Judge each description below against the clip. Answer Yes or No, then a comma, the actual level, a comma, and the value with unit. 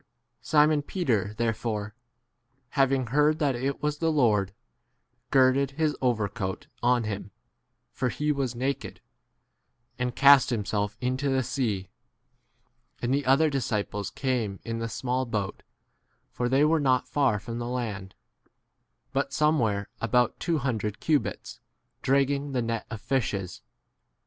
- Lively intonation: No, average, 4.3 semitones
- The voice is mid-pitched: No, low, 125 Hz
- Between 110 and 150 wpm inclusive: Yes, average, 140 wpm